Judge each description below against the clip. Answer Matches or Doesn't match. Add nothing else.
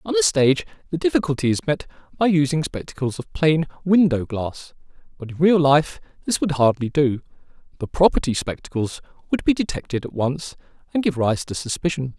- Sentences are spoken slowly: Doesn't match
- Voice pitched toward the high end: Doesn't match